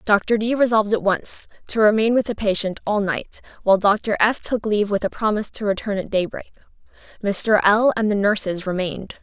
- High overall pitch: Yes, high, 210 Hz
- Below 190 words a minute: No, average, 195 wpm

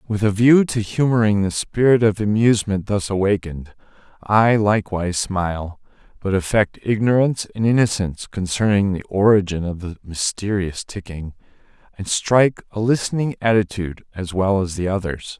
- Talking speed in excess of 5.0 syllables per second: Yes, 5.2 syllables/s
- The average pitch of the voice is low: Yes, low, 100 Hz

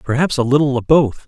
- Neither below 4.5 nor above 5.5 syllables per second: No, 6.0 syllables/s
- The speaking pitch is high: No, low, 135 Hz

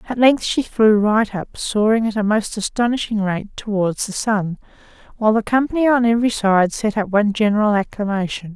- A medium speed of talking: Yes, average, 180 wpm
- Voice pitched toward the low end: No, high, 215 Hz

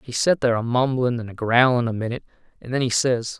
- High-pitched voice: No, low, 120 Hz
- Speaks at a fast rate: Yes, fast, 245 wpm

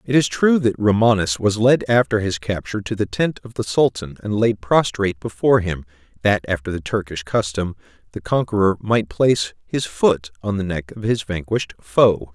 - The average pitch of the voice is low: Yes, low, 105 Hz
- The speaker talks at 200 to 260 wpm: No, average, 190 wpm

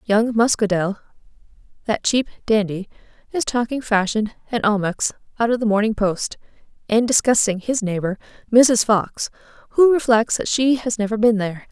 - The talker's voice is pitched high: Yes, high, 220 Hz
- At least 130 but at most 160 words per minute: Yes, average, 150 wpm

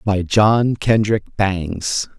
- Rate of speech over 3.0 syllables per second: No, 2.6 syllables/s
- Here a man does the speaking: Yes, male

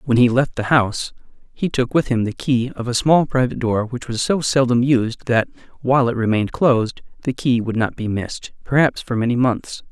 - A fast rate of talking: Yes, fast, 220 wpm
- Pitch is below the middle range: Yes, low, 125 Hz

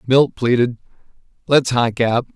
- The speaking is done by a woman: No, male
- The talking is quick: No, slow, 125 wpm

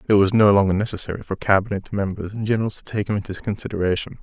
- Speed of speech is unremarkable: No, fast, 215 wpm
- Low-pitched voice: Yes, low, 100 Hz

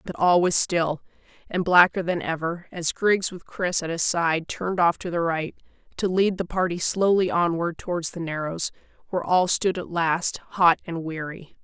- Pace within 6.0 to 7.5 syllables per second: No, 4.7 syllables/s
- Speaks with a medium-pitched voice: Yes, medium, 170 Hz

